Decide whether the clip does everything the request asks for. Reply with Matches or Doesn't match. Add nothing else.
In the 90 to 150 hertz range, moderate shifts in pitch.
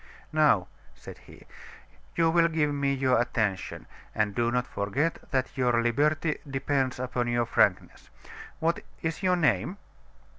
Matches